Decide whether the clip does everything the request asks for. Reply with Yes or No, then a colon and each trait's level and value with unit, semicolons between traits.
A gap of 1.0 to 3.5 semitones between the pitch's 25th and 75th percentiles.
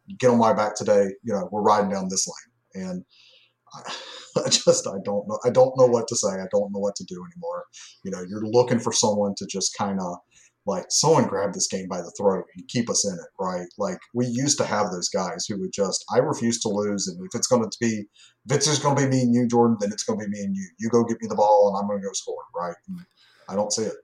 No: average, 4.4 semitones